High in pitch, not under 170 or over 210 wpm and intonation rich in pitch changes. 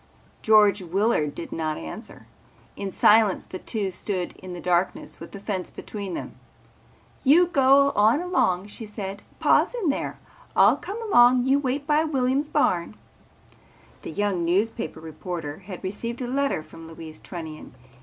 No: high, 205 Hz; average, 155 wpm; wide, 6.7 semitones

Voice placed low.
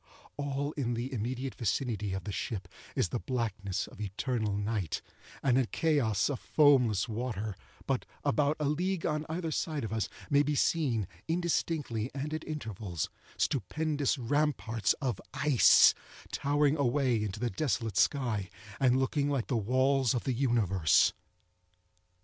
Yes: low, 125 Hz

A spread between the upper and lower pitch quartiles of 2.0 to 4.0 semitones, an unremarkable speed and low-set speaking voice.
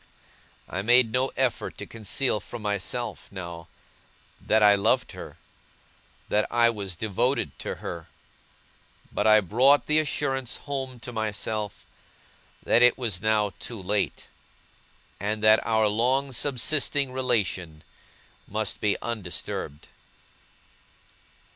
No: average, 3.7 semitones; slow, 115 wpm; low, 110 Hz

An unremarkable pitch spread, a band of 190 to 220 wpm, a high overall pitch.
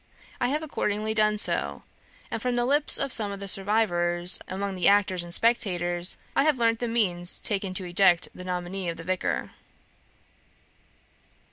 No: average, 4.2 semitones; average, 165 wpm; high, 195 Hz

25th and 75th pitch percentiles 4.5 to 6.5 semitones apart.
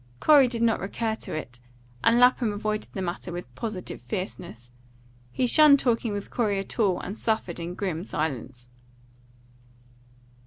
Yes: average, 5.0 semitones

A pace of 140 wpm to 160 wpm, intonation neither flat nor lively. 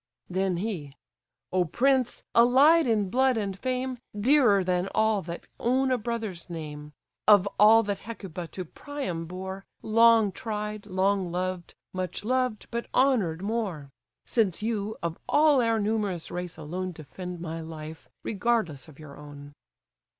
Yes: average, 145 wpm; average, 5.0 semitones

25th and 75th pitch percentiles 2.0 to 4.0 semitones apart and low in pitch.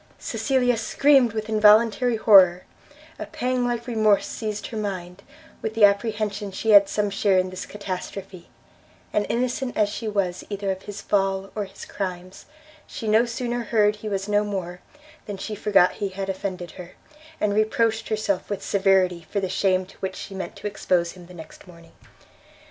No: narrow, 2.5 semitones; high, 205 Hz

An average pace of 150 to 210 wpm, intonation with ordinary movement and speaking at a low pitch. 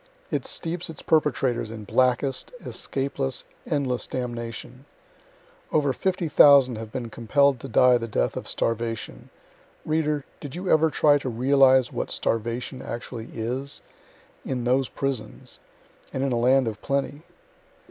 No: slow, 135 wpm; average, 3.1 semitones; low, 130 Hz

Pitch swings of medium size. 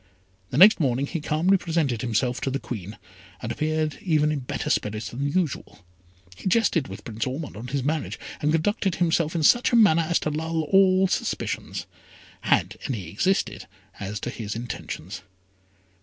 No: wide, 5.7 semitones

